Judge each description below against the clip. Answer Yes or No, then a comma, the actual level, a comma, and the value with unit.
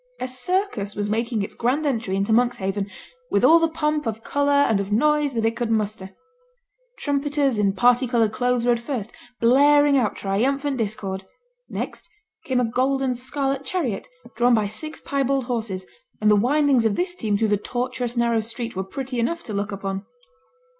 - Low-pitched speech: No, high, 240 Hz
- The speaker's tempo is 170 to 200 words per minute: Yes, average, 180 wpm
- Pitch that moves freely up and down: No, average, 4.5 semitones